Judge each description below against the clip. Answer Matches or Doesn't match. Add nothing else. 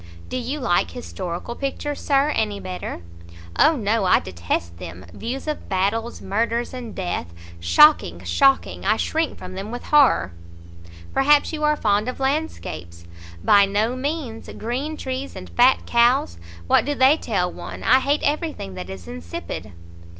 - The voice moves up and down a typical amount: Doesn't match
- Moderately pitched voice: Doesn't match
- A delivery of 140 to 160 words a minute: Matches